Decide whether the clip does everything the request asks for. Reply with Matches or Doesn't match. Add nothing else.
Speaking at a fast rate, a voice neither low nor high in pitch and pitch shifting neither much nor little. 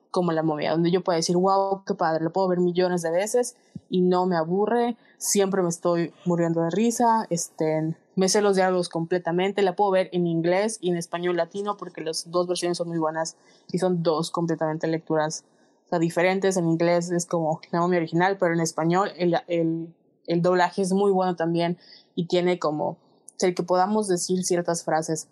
Doesn't match